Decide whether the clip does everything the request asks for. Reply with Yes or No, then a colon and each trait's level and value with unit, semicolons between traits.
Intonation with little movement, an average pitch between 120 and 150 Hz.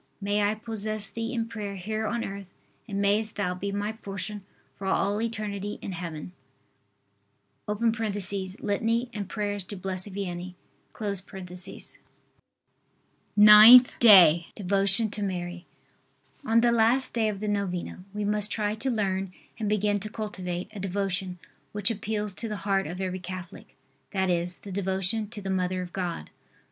No: narrow, 2.3 semitones; high, 200 Hz